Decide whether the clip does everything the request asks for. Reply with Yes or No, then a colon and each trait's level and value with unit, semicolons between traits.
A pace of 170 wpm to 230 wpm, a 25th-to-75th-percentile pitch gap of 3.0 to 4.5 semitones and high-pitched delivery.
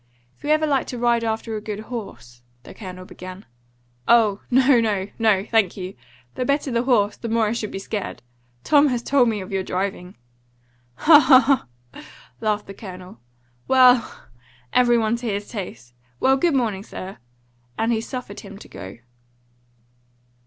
Yes: average, 175 wpm; average, 4.2 semitones; high, 220 Hz